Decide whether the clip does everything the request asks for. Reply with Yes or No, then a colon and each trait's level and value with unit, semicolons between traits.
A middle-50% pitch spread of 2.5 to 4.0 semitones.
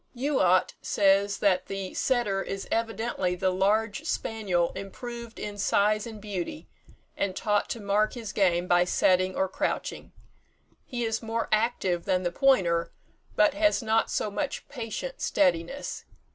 Yes: average, 3.5 semitones